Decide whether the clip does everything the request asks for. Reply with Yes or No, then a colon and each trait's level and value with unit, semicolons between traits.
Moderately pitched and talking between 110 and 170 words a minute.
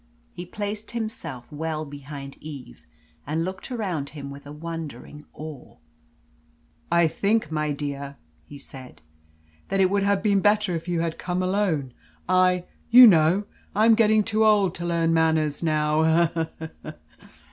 Yes: medium, 165 Hz; average, 160 wpm